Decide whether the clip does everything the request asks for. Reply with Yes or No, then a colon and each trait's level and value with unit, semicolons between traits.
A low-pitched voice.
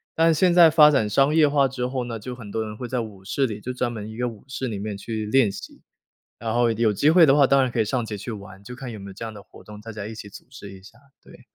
Yes: low, 115 Hz